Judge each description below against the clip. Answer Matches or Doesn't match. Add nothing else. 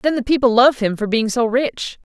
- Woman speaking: Matches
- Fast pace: Matches